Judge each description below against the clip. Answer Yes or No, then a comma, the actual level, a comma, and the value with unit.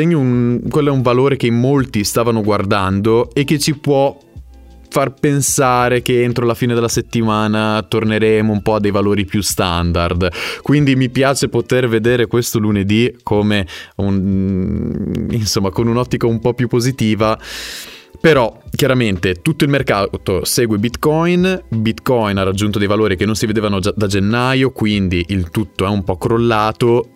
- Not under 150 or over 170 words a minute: Yes, average, 155 wpm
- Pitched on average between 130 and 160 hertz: No, low, 115 Hz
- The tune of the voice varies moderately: Yes, average, 3.3 semitones